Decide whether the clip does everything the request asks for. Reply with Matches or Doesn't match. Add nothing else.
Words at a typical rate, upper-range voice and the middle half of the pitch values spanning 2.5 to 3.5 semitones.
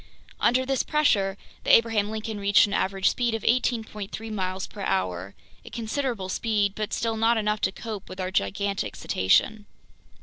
Matches